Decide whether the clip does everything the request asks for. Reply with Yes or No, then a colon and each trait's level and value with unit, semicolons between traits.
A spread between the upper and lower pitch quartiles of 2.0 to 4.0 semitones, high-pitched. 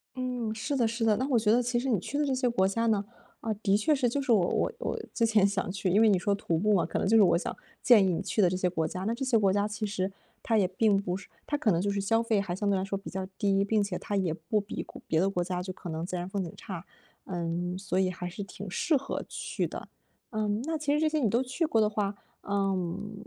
Yes: average, 3.5 semitones; high, 205 Hz